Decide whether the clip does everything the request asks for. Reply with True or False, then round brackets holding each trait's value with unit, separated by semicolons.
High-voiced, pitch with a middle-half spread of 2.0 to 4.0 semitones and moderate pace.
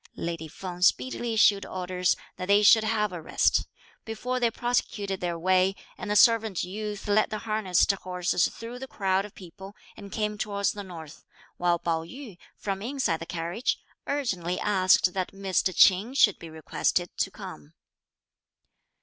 True (195 Hz; 3.2 semitones; 160 wpm)